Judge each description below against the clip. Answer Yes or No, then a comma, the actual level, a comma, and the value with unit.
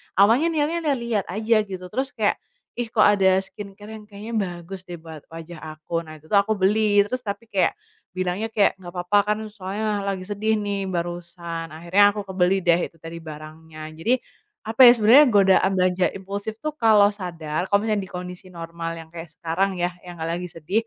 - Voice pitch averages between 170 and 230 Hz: Yes, high, 190 Hz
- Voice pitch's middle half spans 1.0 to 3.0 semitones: No, average, 3.6 semitones